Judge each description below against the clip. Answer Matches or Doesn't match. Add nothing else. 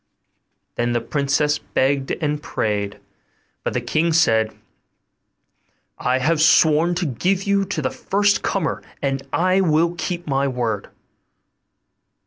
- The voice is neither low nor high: Matches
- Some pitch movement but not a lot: Matches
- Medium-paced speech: Doesn't match